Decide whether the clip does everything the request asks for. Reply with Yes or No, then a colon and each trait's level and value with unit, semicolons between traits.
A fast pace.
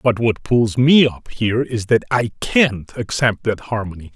No: average, 190 wpm